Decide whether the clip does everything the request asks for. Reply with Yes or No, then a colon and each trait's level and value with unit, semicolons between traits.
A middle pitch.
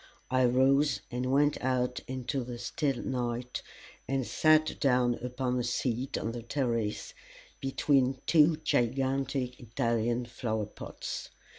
No: low, 125 Hz